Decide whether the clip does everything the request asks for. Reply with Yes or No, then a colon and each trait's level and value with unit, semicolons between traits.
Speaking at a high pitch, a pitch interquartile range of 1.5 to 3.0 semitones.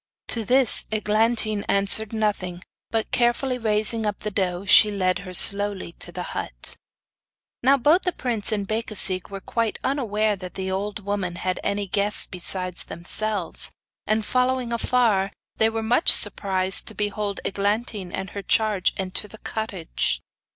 Yes: high, 210 Hz; average, 2.7 semitones